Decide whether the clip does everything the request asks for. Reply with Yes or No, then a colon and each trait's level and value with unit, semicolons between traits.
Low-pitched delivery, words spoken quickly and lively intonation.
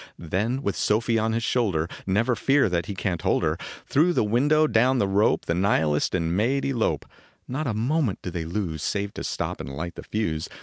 Yes: low, 105 Hz; fast, 215 wpm; wide, 6.2 semitones